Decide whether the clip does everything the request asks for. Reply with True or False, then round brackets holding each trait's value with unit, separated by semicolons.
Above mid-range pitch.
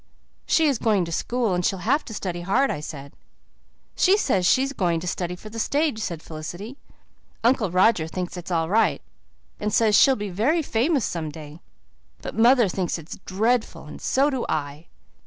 True (205 Hz)